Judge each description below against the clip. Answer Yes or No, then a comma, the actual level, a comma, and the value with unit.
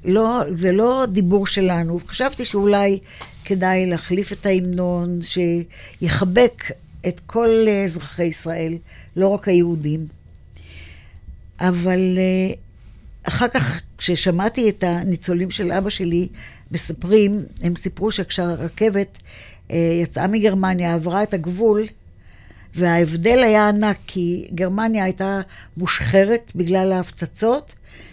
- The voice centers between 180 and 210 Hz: Yes, medium, 185 Hz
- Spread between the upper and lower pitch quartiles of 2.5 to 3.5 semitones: Yes, average, 3.0 semitones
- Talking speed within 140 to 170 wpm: No, slow, 100 wpm